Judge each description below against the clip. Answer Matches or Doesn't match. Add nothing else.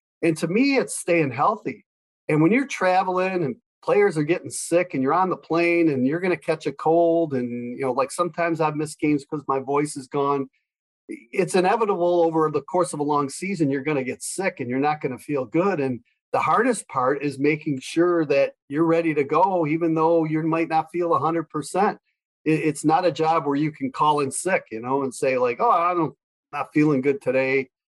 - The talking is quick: Matches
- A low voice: Doesn't match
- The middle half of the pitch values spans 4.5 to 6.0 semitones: Doesn't match